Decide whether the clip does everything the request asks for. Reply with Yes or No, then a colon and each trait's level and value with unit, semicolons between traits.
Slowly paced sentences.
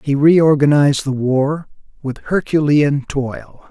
Yes: slow, 115 wpm